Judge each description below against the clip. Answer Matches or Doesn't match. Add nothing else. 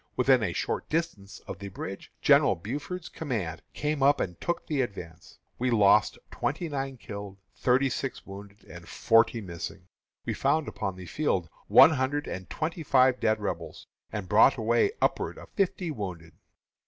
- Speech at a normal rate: Matches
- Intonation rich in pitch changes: Matches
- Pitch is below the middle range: Matches